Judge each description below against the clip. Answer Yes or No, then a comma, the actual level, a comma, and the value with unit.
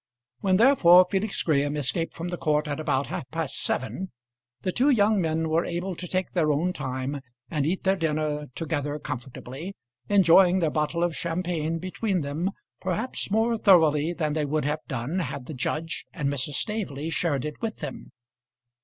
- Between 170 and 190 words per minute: Yes, average, 175 wpm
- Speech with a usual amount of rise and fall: Yes, average, 3.9 semitones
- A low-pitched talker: No, medium, 160 Hz